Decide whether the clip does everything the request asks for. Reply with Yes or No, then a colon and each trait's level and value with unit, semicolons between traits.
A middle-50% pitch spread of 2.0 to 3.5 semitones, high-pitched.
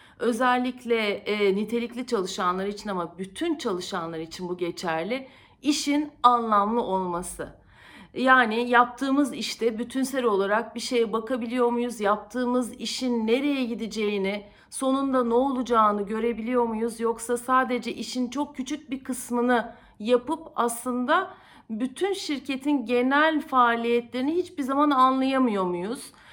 Yes: average, 2.9 semitones; high, 240 Hz